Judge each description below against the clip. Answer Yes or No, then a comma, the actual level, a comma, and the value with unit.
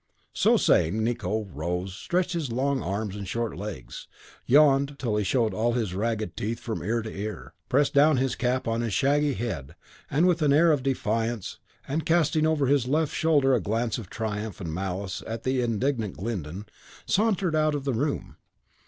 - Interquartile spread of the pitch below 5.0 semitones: No, average, 5.3 semitones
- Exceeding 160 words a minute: Yes, average, 180 wpm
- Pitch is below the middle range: Yes, low, 120 Hz